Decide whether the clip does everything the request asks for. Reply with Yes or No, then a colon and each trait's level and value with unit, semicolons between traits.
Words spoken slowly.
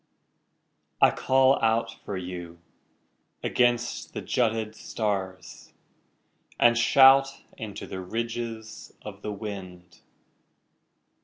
Yes: slow, 90 wpm